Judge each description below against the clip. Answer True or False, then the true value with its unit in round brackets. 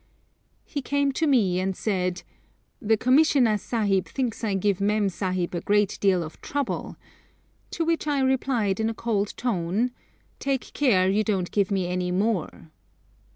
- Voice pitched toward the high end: True (210 Hz)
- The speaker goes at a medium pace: True (155 wpm)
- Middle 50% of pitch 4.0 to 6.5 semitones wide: True (5.2 semitones)